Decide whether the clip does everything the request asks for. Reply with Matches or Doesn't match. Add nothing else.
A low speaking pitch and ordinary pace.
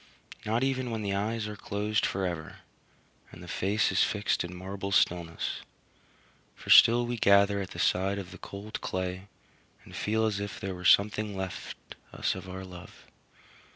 Matches